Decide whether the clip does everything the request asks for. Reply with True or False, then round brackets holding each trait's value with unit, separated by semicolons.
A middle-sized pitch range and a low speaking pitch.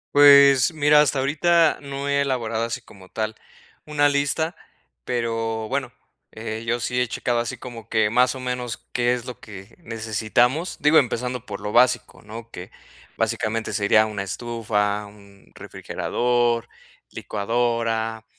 True (3.1 semitones; 120 Hz)